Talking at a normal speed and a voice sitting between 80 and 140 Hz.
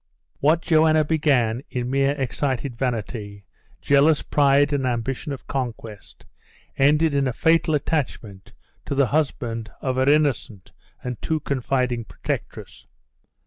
No: slow, 125 wpm; low, 135 Hz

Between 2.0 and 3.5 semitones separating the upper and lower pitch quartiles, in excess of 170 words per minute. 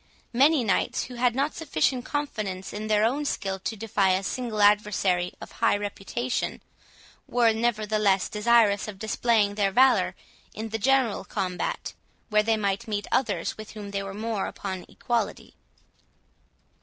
No: average, 3.0 semitones; average, 155 wpm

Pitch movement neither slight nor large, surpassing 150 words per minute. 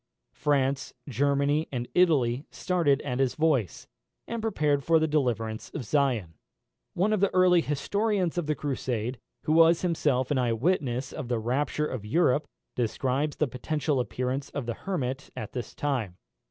Yes: average, 4.1 semitones; average, 160 wpm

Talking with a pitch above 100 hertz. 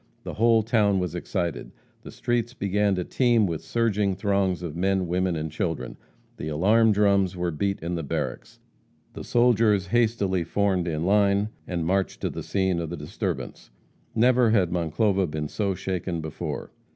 No: very low, 95 Hz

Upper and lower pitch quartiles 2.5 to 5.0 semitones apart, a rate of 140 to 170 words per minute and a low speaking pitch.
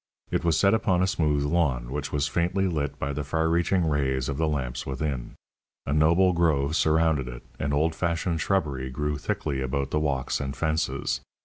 No: average, 3.2 semitones; average, 190 wpm; very low, 75 Hz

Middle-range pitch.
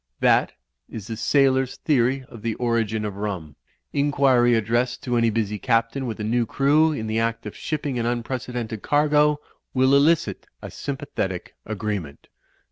No: low, 120 Hz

